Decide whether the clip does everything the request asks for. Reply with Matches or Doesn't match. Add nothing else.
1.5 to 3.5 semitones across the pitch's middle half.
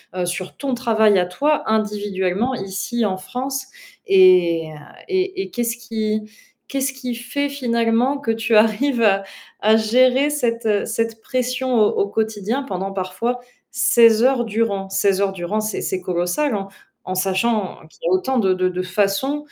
Doesn't match